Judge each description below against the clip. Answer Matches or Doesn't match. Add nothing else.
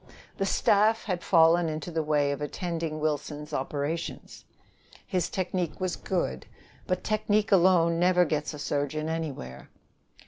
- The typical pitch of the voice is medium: Matches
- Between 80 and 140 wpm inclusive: Matches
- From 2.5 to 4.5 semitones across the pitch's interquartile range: Matches